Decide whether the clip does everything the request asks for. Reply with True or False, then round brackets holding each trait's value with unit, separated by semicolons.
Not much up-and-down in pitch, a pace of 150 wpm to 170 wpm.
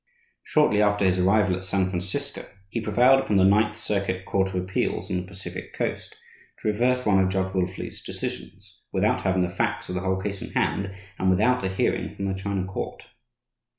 False (2.1 semitones; 195 wpm)